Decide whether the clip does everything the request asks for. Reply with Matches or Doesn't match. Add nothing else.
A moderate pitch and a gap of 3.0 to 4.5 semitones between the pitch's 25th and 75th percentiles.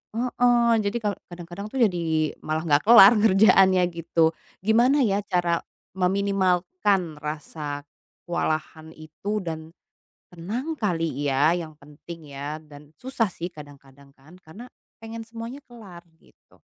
Doesn't match